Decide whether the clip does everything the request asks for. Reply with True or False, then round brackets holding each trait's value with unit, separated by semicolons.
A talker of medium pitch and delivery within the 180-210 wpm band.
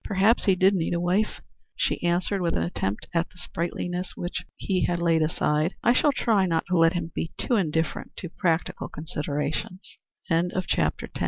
True (175 Hz; 200 wpm)